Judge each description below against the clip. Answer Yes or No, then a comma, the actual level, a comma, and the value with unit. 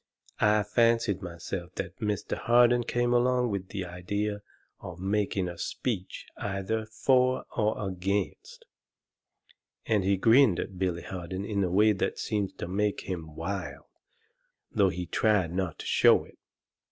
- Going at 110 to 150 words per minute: Yes, average, 145 wpm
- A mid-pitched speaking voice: No, low, 100 Hz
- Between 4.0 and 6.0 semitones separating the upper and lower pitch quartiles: No, average, 2.9 semitones